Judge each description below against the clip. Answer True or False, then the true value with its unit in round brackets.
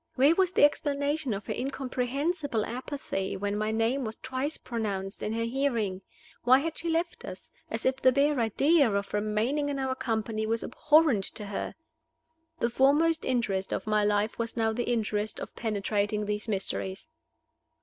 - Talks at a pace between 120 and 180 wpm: True (170 wpm)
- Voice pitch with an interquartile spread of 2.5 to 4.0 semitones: False (4.8 semitones)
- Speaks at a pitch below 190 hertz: False (235 Hz)